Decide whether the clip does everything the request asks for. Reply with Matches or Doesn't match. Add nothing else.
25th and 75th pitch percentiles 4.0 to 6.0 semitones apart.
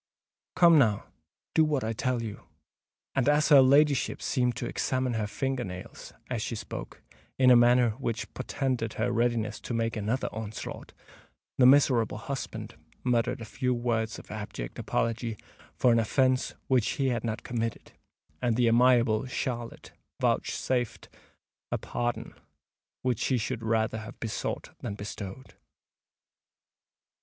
Doesn't match